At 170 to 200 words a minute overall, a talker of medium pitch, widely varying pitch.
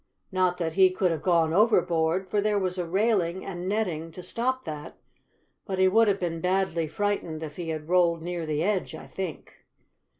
No: average, 195 wpm; medium, 180 Hz; average, 2.8 semitones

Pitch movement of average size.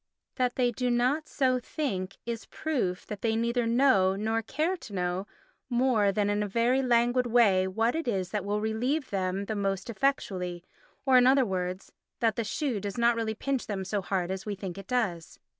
Yes: average, 4.4 semitones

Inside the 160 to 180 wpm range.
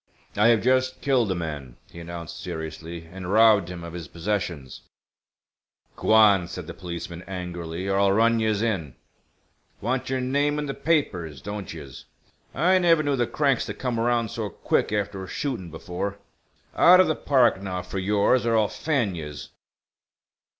Yes: average, 170 wpm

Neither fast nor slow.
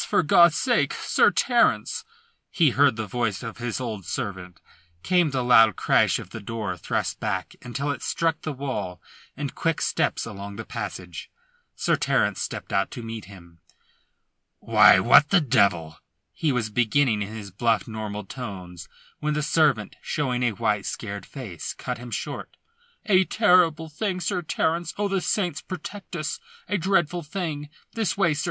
Yes: average, 170 wpm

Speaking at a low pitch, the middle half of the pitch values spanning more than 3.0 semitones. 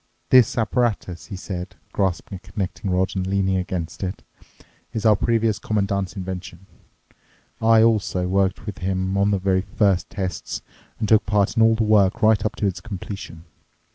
No: low, 100 Hz; narrow, 2.5 semitones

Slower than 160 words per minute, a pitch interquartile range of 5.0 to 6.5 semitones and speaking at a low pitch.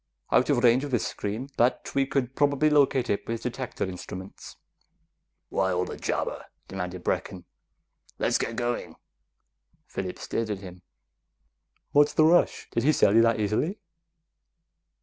Yes: average, 150 wpm; wide, 5.4 semitones; low, 120 Hz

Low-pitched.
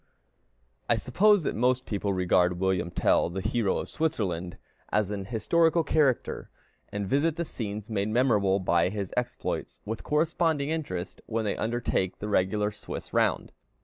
Yes: low, 105 Hz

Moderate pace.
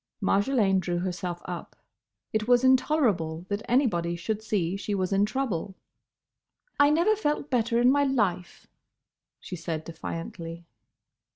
No: slow, 130 wpm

